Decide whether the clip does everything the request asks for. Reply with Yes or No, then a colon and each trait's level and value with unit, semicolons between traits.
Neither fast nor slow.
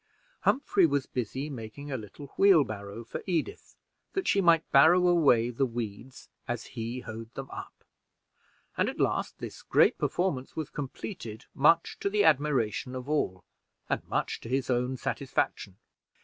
Yes: average, 150 wpm